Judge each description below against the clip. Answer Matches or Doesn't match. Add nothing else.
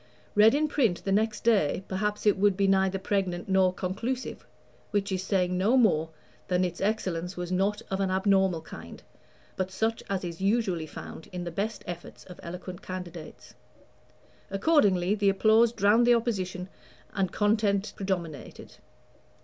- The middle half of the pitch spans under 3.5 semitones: Matches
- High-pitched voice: Matches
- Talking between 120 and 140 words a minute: Doesn't match